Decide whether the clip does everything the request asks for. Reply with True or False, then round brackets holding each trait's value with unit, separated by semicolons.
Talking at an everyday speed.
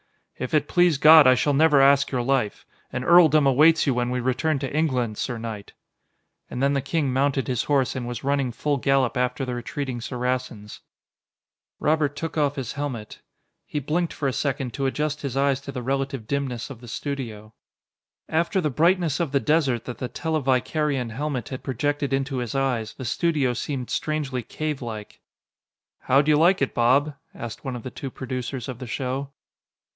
True (185 wpm)